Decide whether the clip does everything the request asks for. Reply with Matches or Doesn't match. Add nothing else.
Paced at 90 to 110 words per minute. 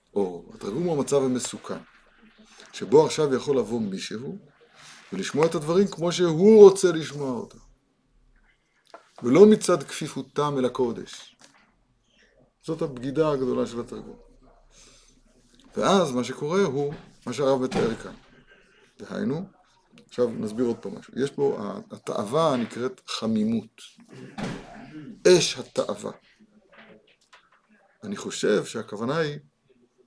Matches